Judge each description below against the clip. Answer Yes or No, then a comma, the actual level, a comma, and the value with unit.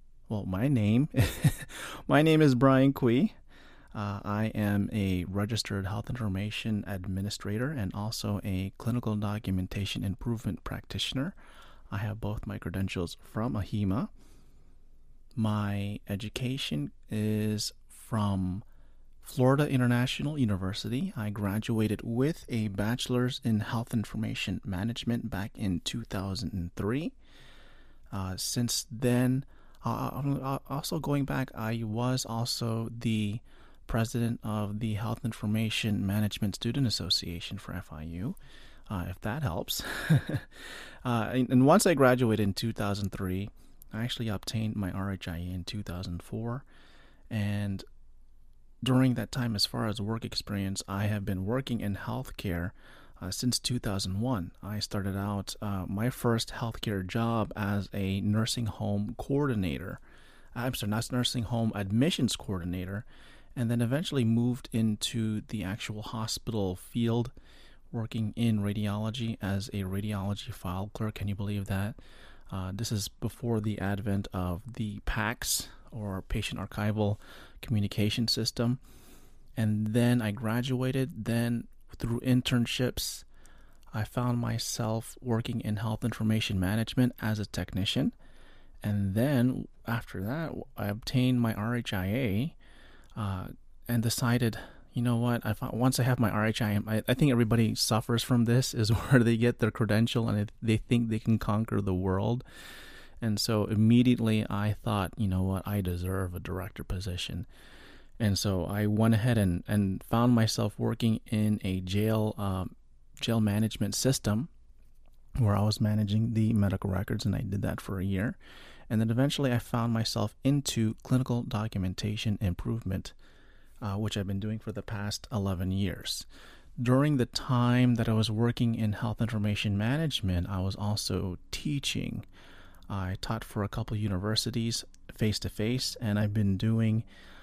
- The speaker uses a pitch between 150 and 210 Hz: No, low, 110 Hz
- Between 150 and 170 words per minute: No, slow, 135 wpm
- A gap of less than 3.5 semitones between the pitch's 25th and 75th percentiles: Yes, average, 3.1 semitones